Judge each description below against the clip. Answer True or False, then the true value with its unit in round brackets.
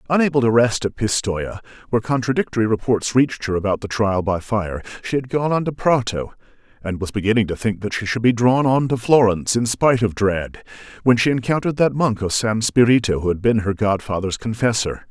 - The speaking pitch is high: False (115 Hz)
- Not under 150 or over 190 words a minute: False (205 wpm)